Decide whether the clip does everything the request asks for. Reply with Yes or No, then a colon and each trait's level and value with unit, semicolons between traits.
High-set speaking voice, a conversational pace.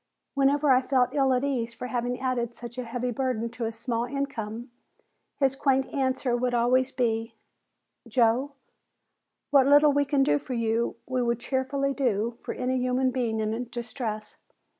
Yes: very high, 250 Hz; average, 165 wpm